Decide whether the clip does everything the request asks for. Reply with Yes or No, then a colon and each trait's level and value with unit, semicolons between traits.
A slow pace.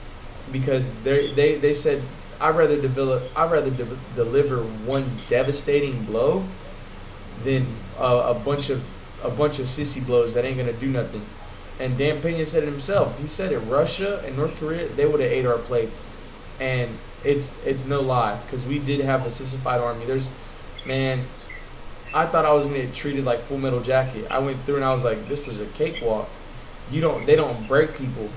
No: average, 190 wpm